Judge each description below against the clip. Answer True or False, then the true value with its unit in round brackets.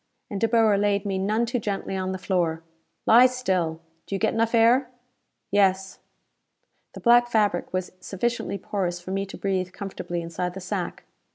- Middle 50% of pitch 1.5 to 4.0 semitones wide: True (3.4 semitones)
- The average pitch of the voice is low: False (195 Hz)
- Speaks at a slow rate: False (175 wpm)